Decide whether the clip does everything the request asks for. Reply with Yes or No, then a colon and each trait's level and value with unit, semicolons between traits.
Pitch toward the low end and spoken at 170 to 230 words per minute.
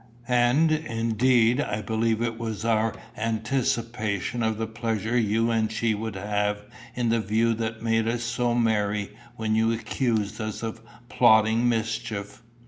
No: low, 115 Hz; average, 145 wpm